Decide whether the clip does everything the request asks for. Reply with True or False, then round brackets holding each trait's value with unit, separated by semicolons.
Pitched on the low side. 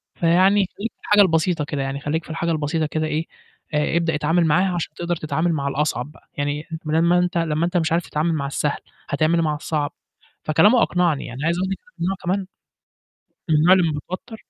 False (160 Hz)